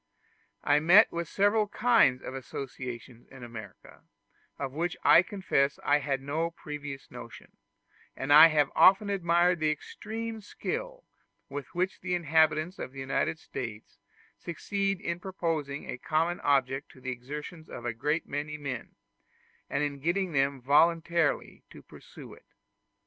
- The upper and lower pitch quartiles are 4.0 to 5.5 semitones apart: Yes, average, 4.3 semitones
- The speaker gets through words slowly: No, average, 145 wpm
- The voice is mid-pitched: Yes, medium, 155 Hz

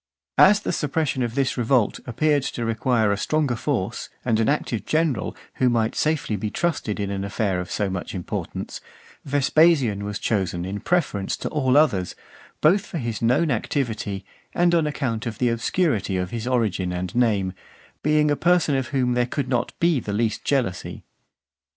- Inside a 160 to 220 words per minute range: Yes, average, 180 wpm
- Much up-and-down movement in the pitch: Yes, wide, 6.1 semitones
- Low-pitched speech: Yes, low, 120 Hz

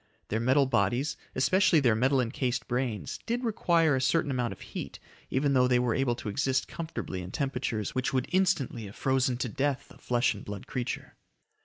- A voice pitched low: Yes, low, 130 Hz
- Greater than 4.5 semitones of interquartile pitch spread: No, average, 2.8 semitones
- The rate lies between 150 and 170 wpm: No, average, 190 wpm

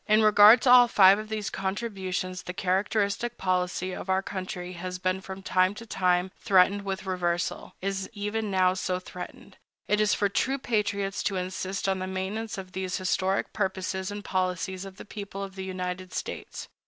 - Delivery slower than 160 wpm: No, average, 180 wpm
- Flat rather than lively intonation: Yes, narrow, 1.7 semitones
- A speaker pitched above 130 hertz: Yes, high, 190 Hz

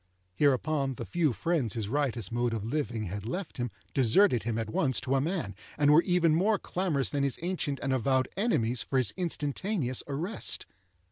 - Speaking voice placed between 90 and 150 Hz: Yes, medium, 140 Hz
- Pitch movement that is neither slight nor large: No, wide, 5.7 semitones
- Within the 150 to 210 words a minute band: Yes, average, 185 wpm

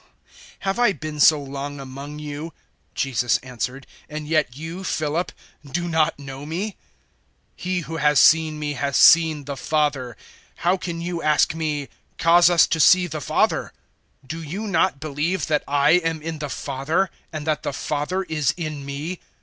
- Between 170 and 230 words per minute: Yes, average, 175 wpm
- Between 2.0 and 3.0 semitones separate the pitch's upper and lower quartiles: Yes, average, 2.7 semitones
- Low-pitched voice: No, medium, 155 Hz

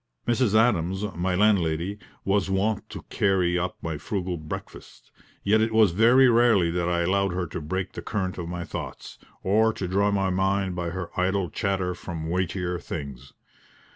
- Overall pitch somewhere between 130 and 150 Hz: No, very low, 95 Hz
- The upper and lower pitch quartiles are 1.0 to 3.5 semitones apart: Yes, average, 2.7 semitones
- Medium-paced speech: Yes, average, 170 wpm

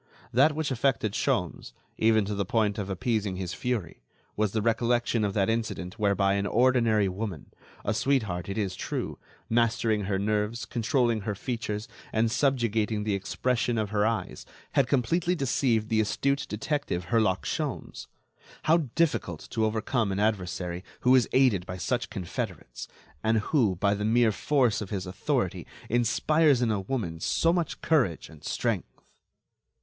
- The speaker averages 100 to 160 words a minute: Yes, average, 155 wpm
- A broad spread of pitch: No, average, 3.6 semitones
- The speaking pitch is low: Yes, low, 110 Hz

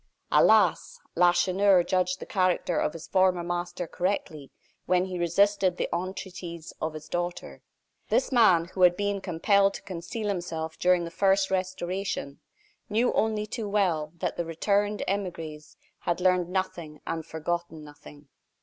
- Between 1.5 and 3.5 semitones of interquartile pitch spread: Yes, average, 2.7 semitones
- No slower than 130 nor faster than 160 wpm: Yes, average, 145 wpm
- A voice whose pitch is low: No, medium, 180 Hz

